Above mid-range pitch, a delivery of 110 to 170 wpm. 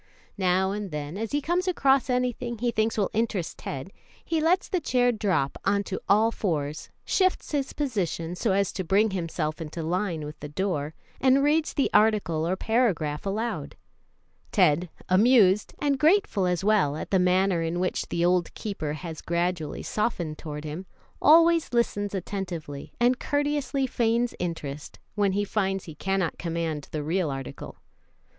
Yes: high, 195 Hz; average, 165 wpm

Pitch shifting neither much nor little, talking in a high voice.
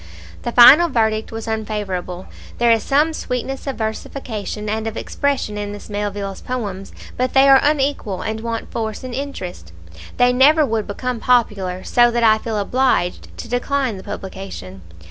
Yes: average, 3.7 semitones; high, 225 Hz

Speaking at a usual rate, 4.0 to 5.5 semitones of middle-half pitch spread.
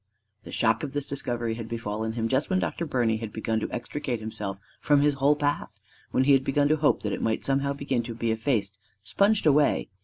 No: fast, 220 wpm; average, 4.3 semitones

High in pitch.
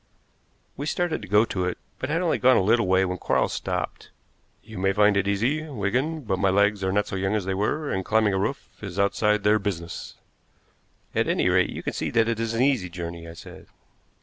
No: low, 105 Hz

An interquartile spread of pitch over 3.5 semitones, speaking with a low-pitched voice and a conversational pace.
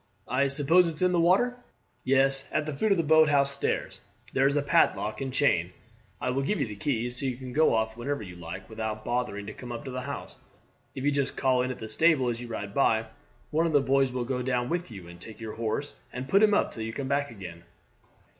No: average, 4.2 semitones; low, 130 Hz; fast, 250 wpm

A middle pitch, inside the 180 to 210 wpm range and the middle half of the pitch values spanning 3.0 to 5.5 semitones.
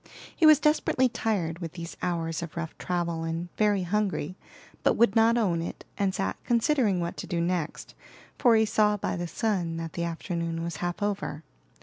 Yes: medium, 175 Hz; average, 190 wpm; average, 4.1 semitones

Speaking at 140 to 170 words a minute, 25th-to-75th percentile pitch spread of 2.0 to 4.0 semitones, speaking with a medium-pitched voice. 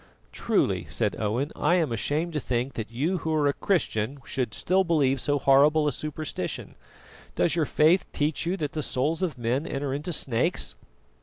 No: average, 180 wpm; average, 3.5 semitones; medium, 145 Hz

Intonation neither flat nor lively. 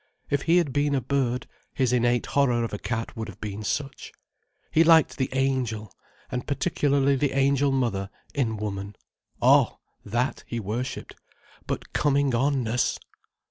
Yes: average, 3.7 semitones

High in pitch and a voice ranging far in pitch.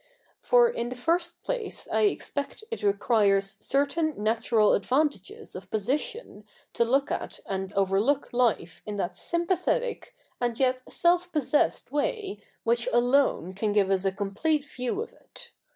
Yes: high, 245 Hz; wide, 7.5 semitones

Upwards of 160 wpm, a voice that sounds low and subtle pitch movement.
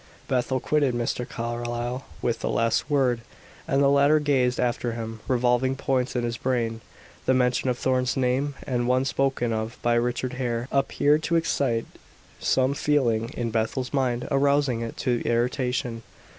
No: average, 155 wpm; low, 125 Hz; narrow, 2.2 semitones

